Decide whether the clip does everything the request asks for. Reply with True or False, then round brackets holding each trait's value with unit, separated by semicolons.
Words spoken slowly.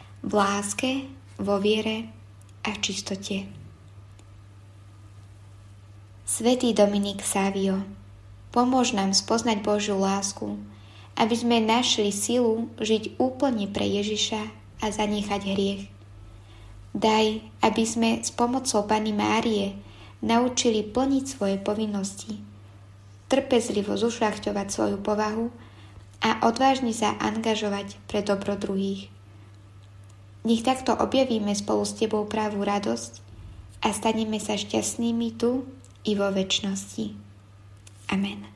True (100 wpm)